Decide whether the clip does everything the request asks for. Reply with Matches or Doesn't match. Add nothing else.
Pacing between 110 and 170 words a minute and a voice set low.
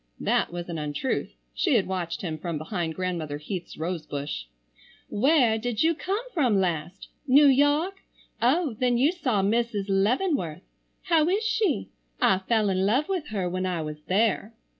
Doesn't match